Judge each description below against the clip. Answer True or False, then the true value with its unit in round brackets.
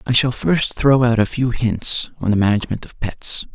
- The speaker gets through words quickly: True (220 wpm)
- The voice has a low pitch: True (115 Hz)